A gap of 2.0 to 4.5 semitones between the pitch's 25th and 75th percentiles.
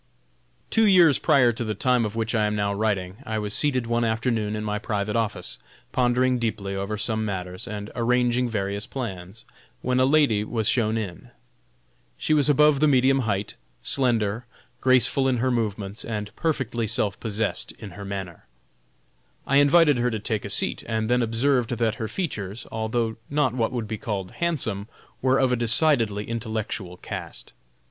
Yes: average, 3.3 semitones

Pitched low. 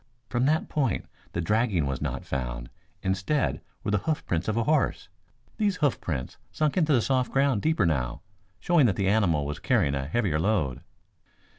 Yes: low, 105 Hz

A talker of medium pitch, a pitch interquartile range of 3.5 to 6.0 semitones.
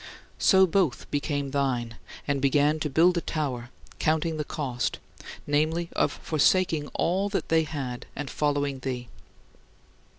No: medium, 145 Hz; average, 3.0 semitones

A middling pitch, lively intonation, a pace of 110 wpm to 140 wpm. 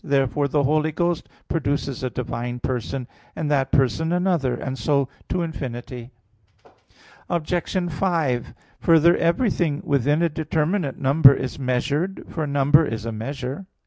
No: medium, 145 Hz; average, 4.0 semitones; slow, 135 wpm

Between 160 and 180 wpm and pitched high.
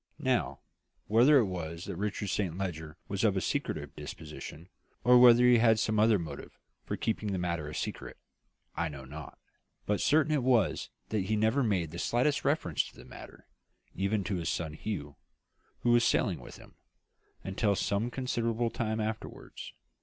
No: average, 175 wpm; low, 105 Hz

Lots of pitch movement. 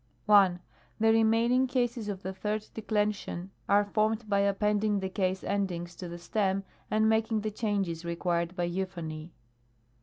No: average, 2.9 semitones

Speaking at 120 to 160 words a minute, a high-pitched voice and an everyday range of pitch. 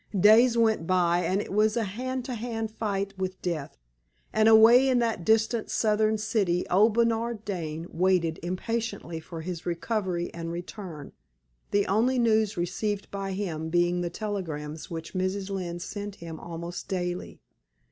Yes: average, 155 wpm; high, 195 Hz; average, 4.1 semitones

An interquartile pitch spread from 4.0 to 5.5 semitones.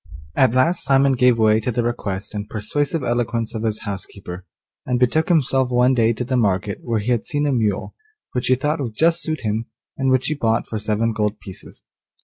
No: average, 3.5 semitones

